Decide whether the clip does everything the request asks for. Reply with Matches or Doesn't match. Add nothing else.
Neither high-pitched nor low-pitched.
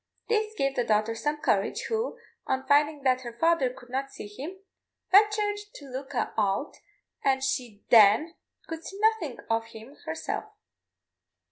Doesn't match